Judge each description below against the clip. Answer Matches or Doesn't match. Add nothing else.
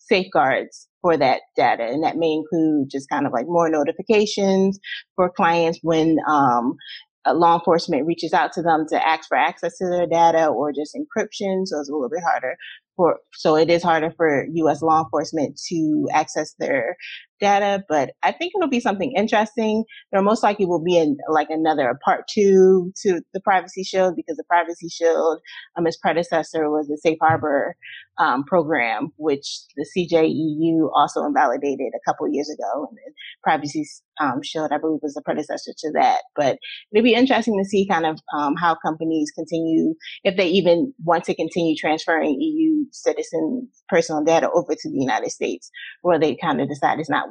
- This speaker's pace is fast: Doesn't match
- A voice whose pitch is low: Doesn't match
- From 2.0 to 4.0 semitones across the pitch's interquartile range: Doesn't match